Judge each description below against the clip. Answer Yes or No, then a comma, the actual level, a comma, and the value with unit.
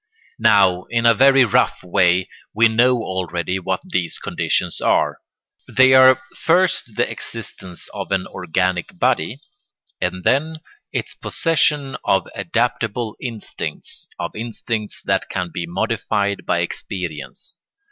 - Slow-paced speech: Yes, slow, 125 wpm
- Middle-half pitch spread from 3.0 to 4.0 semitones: No, average, 5.1 semitones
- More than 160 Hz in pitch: No, low, 105 Hz